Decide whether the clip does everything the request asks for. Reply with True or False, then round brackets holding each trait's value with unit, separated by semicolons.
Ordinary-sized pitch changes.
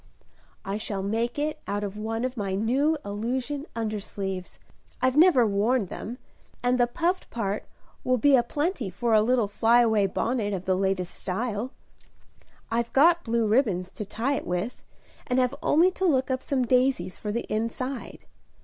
True (4.0 semitones)